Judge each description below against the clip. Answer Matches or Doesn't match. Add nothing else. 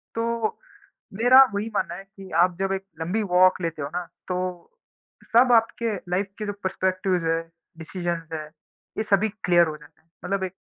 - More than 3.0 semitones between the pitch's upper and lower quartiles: Matches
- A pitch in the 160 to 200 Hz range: Matches